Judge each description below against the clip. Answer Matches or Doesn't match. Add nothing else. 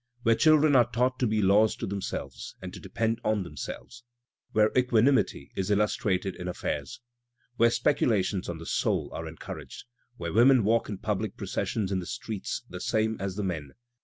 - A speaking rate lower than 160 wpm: Doesn't match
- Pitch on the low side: Matches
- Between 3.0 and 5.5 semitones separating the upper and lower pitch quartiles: Matches